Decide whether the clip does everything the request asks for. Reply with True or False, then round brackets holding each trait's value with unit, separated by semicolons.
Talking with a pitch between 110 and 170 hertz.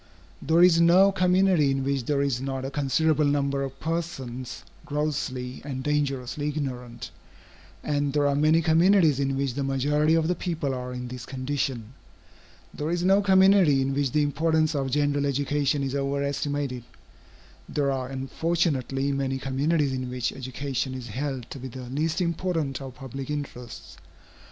True (140 Hz)